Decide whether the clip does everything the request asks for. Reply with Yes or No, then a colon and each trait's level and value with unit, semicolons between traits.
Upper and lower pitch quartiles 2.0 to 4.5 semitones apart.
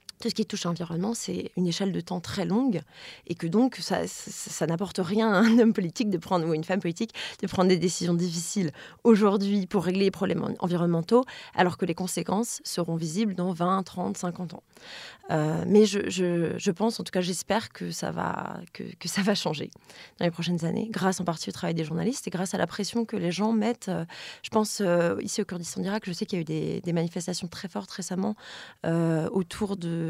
Yes: average, 3.3 semitones